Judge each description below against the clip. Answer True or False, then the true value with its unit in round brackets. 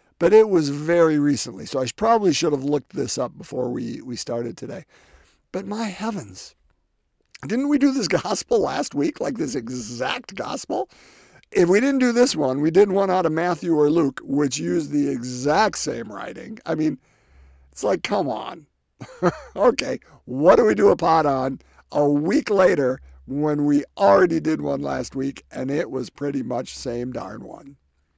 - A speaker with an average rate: True (180 wpm)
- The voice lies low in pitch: False (145 Hz)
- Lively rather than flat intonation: True (6.8 semitones)